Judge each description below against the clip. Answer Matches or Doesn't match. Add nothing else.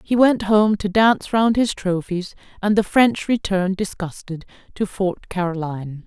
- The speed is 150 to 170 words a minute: Matches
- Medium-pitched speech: Doesn't match